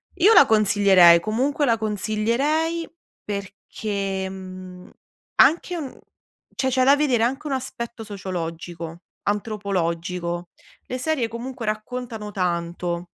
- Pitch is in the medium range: No, high, 215 Hz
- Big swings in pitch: Yes, wide, 5.7 semitones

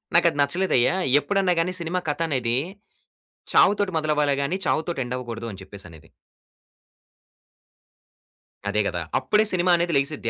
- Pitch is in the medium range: Yes, medium, 150 Hz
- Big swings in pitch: Yes, wide, 6.8 semitones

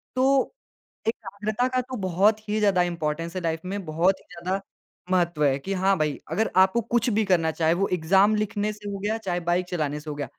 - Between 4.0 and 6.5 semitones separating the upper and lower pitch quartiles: Yes, average, 4.3 semitones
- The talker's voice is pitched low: No, high, 190 Hz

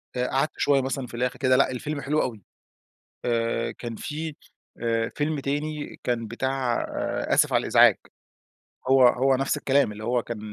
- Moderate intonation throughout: Yes, average, 3.0 semitones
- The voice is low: Yes, low, 130 Hz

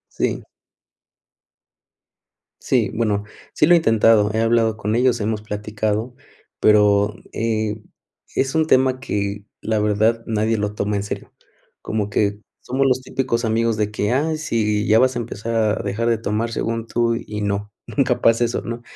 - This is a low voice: Yes, low, 110 Hz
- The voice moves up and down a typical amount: No, narrow, 2.0 semitones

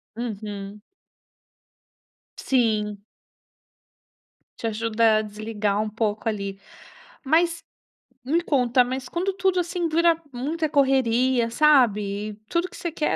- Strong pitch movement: Yes, wide, 6.7 semitones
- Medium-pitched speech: No, high, 240 Hz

